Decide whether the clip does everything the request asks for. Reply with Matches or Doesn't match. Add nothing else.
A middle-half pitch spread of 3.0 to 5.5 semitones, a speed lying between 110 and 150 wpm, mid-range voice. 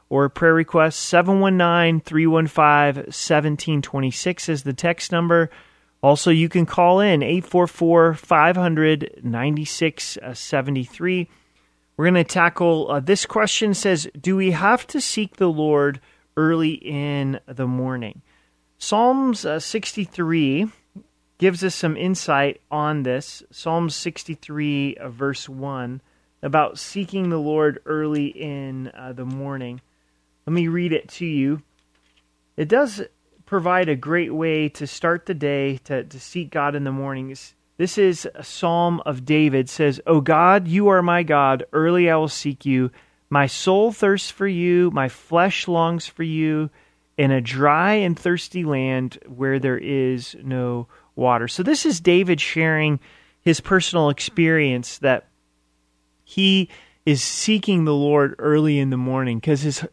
Matches